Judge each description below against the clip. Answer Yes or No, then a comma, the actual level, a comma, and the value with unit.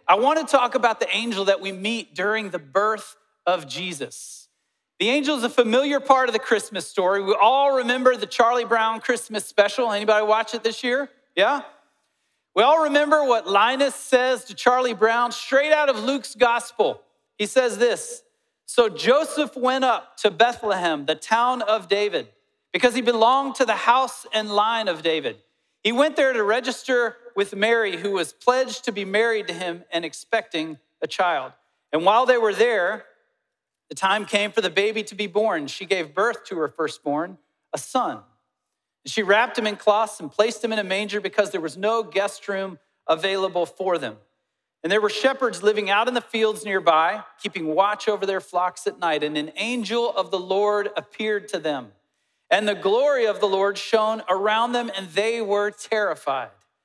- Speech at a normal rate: Yes, average, 185 wpm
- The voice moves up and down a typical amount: Yes, average, 4.0 semitones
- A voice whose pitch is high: Yes, high, 215 Hz